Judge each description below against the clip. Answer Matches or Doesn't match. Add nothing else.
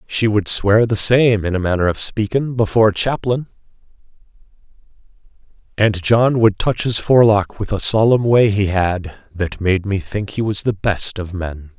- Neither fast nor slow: Matches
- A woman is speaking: Doesn't match